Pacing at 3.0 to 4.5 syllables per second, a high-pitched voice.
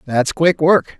No: 3.5 syllables/s; medium, 155 Hz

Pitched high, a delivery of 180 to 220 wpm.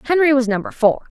Yes: very high, 265 Hz; average, 200 wpm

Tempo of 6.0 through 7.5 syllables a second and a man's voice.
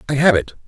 Yes: 7.3 syllables/s; male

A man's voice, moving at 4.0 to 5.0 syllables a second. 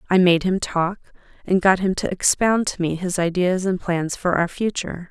No: female; 4.9 syllables/s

